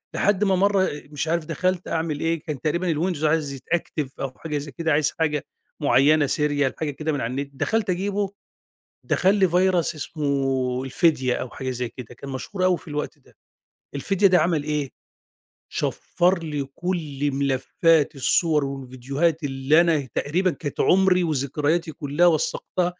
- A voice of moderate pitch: Yes, medium, 155 Hz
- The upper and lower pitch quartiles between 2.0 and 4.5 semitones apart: Yes, average, 3.9 semitones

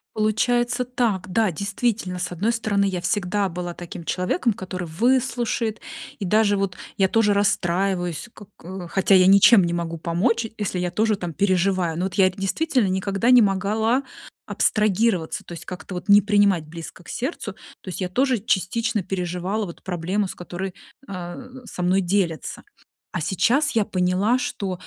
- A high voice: Yes, high, 195 Hz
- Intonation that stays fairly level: No, average, 3.3 semitones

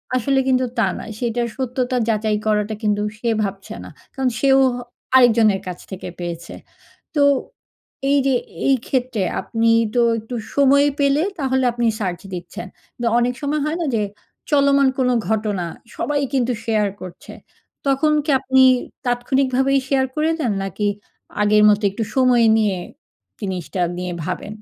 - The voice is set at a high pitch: Yes, high, 245 Hz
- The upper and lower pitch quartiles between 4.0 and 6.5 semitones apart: Yes, average, 4.3 semitones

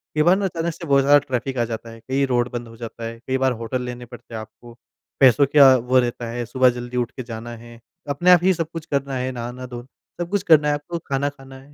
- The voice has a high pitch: No, low, 130 Hz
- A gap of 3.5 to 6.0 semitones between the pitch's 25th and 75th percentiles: No, average, 3.1 semitones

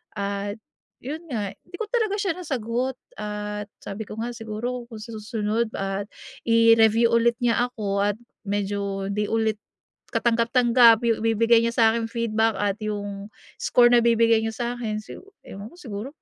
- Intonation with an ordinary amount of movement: No, narrow, 2.3 semitones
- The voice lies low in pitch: No, high, 225 Hz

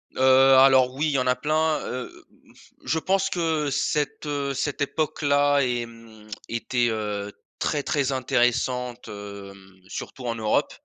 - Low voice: Yes, low, 130 Hz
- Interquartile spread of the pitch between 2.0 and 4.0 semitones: Yes, average, 3.6 semitones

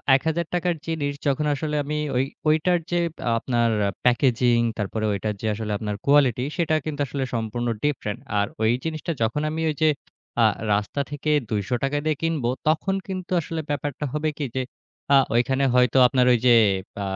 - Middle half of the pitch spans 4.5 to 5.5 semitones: Yes, average, 4.8 semitones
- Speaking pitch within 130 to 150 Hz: Yes, medium, 140 Hz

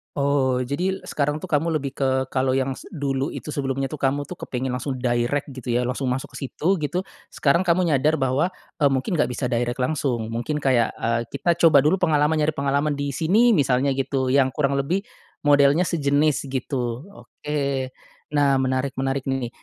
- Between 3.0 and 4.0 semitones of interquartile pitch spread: No, narrow, 2.6 semitones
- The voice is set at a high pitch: No, medium, 140 Hz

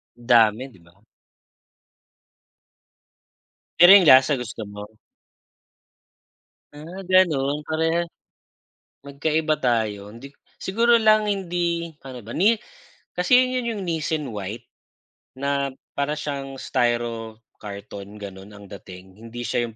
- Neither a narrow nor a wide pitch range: No, wide, 7.3 semitones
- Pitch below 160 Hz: Yes, low, 135 Hz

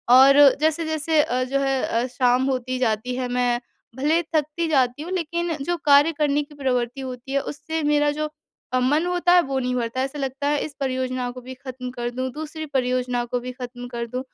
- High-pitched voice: Yes, very high, 265 Hz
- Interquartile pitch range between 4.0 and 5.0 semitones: No, average, 3.0 semitones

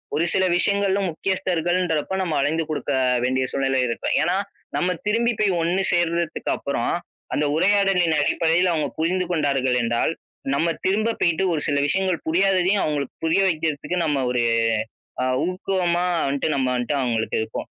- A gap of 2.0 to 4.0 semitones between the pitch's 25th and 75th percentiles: No, average, 4.5 semitones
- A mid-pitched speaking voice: Yes, medium, 170 Hz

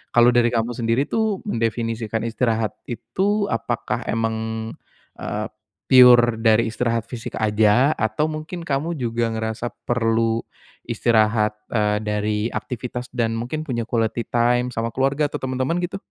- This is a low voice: Yes, low, 115 Hz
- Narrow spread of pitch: Yes, narrow, 2.3 semitones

